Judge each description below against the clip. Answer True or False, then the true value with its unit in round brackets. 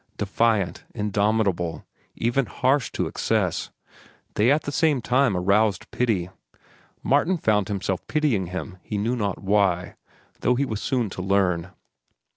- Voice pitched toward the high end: False (105 Hz)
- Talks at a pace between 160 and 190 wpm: False (135 wpm)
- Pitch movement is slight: False (4.6 semitones)